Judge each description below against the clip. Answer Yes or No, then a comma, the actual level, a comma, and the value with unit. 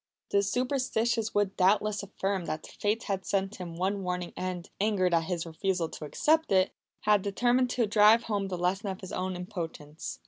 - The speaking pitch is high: Yes, high, 195 Hz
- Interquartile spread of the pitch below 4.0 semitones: Yes, average, 2.8 semitones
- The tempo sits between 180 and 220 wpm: Yes, average, 185 wpm